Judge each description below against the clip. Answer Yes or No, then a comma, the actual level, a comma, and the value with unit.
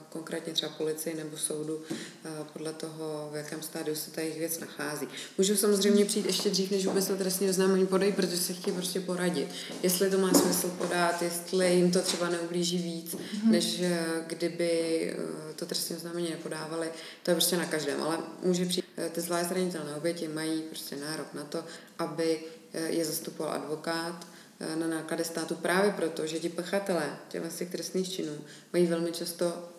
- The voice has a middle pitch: Yes, medium, 170 Hz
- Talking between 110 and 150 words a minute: No, average, 165 wpm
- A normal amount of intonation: No, narrow, 2.2 semitones